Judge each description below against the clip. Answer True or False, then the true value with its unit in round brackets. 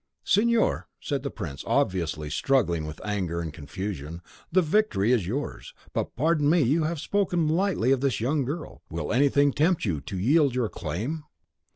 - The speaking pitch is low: True (130 Hz)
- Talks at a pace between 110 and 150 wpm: False (170 wpm)